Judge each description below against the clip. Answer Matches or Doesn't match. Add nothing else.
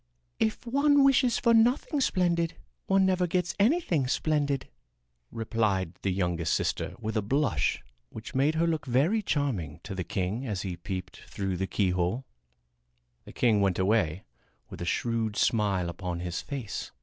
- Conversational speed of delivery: Matches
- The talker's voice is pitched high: Doesn't match